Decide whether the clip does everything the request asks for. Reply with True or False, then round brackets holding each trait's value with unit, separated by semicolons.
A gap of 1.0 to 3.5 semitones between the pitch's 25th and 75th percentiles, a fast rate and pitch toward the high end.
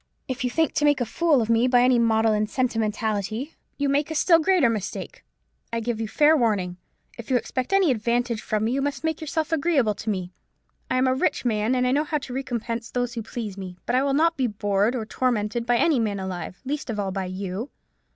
False (4.3 semitones; 230 wpm; 240 Hz)